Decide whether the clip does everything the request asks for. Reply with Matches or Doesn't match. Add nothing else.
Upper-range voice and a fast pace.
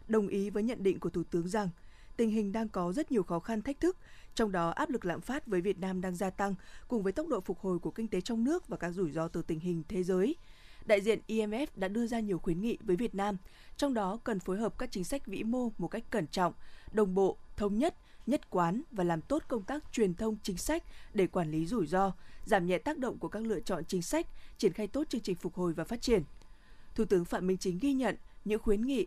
Matches